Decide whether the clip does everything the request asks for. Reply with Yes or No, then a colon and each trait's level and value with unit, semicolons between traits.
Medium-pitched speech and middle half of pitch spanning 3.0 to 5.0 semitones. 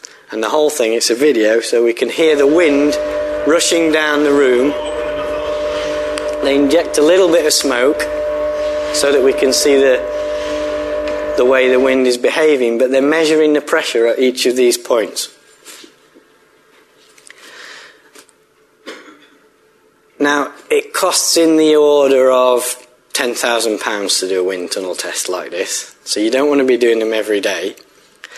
Yes: medium, 150 Hz; average, 4.1 semitones